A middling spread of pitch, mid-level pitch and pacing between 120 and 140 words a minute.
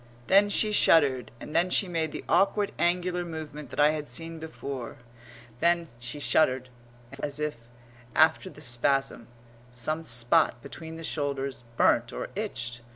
Yes: average, 5.0 semitones; medium, 150 Hz; slow, 135 wpm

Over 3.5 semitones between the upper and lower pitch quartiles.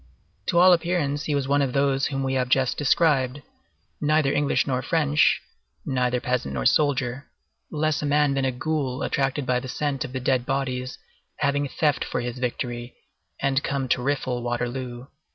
No: narrow, 2.5 semitones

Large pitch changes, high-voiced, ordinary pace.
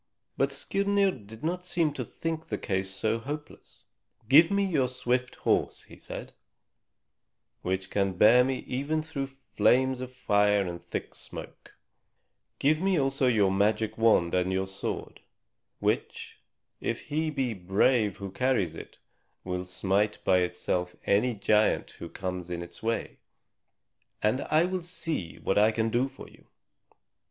No: wide, 6.3 semitones; low, 115 Hz; average, 150 wpm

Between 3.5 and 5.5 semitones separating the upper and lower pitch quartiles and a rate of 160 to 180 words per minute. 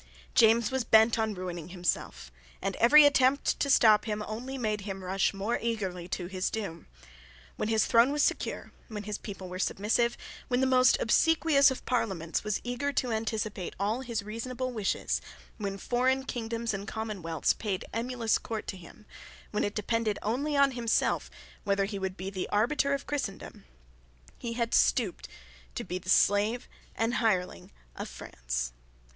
Yes: average, 3.9 semitones; average, 165 wpm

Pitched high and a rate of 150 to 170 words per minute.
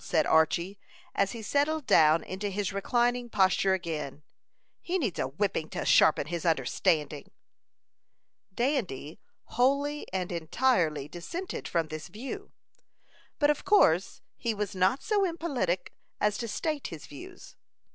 No: high, 195 Hz; slow, 135 wpm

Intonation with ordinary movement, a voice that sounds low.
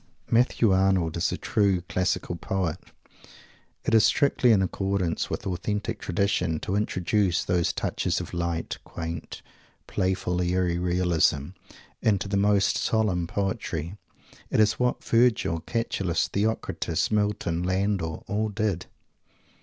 Yes: average, 3.1 semitones; very low, 95 Hz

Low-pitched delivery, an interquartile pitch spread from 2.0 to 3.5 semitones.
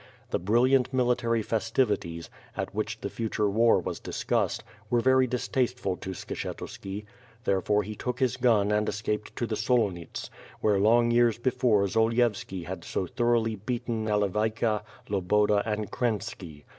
Yes: low, 110 Hz; average, 2.7 semitones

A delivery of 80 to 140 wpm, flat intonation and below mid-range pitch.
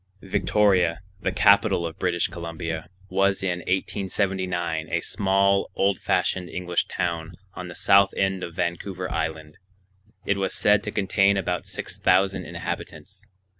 Yes: slow, 135 wpm; narrow, 2.3 semitones; very low, 90 Hz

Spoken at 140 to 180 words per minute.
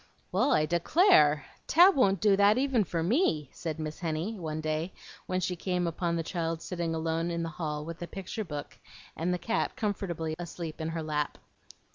No: average, 190 wpm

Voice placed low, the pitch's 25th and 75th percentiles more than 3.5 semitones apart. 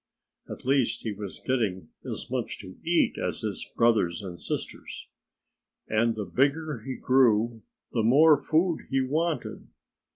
Yes: low, 125 Hz; average, 5.0 semitones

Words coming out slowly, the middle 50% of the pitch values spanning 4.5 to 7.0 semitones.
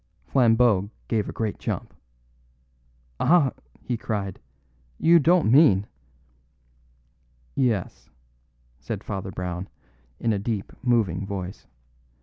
Yes: slow, 105 wpm; average, 5.1 semitones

